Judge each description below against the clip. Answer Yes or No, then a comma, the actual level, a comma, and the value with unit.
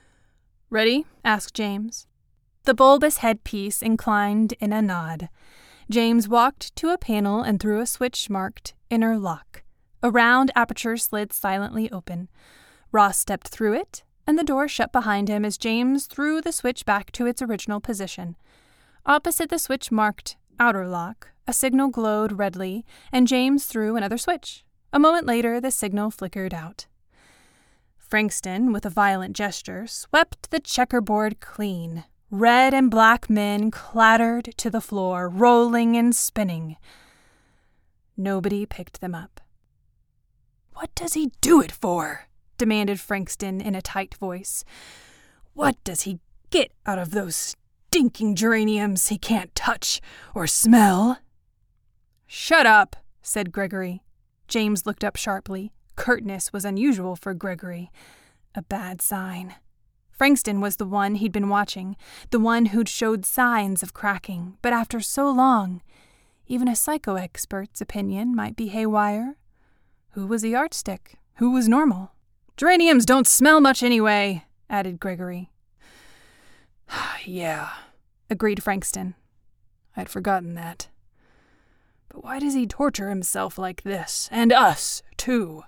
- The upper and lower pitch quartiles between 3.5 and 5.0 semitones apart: Yes, average, 3.9 semitones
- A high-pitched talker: Yes, high, 210 Hz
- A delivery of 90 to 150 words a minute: Yes, slow, 135 wpm